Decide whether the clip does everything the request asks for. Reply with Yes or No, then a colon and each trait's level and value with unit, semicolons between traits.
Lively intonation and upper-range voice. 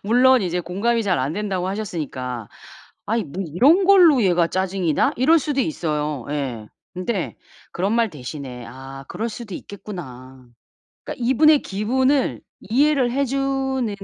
Yes: wide, 9.0 semitones; high, 200 Hz